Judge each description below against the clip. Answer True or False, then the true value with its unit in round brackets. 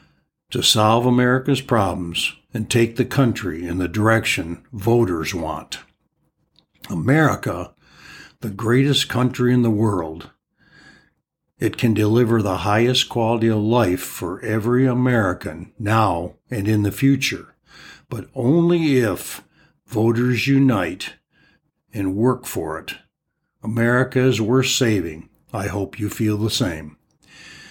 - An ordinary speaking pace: False (120 wpm)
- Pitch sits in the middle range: False (115 Hz)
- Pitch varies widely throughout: False (3.2 semitones)